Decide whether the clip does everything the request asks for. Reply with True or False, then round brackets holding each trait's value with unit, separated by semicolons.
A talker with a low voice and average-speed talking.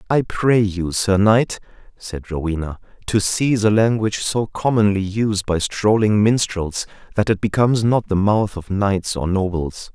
True (100 Hz; 165 wpm)